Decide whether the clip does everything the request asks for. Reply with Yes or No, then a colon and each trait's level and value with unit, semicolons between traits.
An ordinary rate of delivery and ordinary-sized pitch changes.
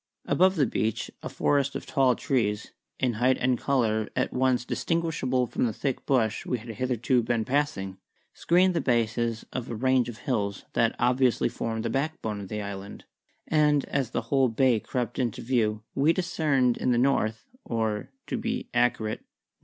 Yes: average, 175 wpm; average, 3.5 semitones